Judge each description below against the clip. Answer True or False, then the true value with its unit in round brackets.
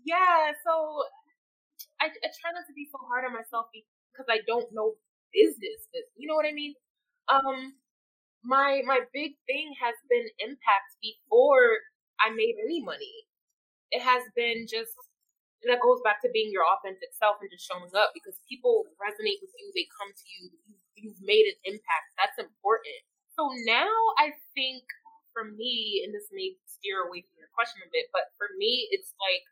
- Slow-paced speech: False (180 wpm)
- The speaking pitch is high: True (290 Hz)